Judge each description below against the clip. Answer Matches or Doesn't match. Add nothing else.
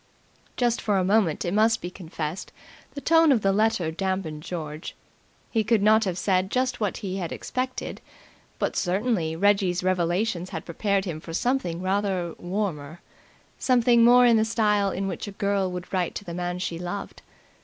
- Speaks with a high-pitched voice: Matches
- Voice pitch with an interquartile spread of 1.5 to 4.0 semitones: Matches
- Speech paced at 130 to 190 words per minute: Matches